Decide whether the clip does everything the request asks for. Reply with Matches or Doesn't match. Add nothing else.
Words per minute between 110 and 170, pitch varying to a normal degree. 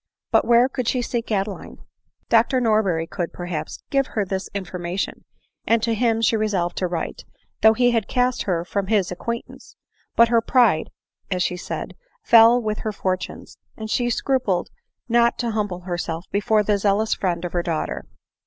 Doesn't match